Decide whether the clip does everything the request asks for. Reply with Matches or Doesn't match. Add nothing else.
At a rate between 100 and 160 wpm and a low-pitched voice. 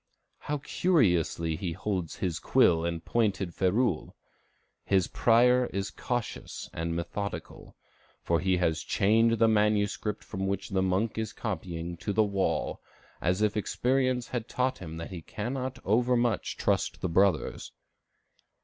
Matches